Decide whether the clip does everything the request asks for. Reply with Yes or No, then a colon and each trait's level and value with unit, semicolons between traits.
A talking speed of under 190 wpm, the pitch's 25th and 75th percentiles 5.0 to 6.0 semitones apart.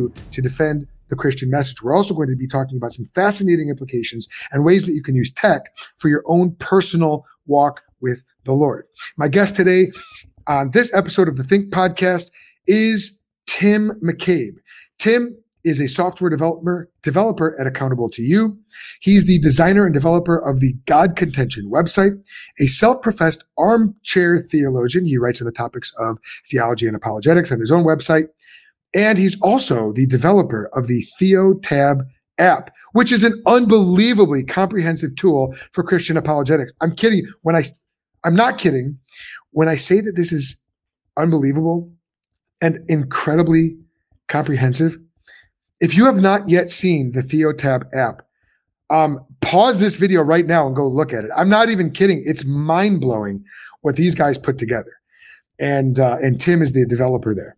Yes: average, 165 wpm; wide, 5.6 semitones